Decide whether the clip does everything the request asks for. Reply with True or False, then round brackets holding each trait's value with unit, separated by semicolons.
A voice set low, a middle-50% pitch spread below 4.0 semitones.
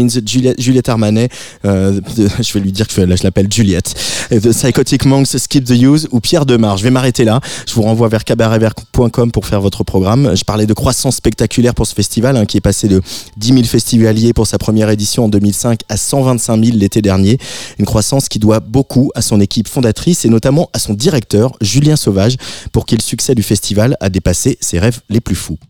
True (115 Hz; 3.3 semitones)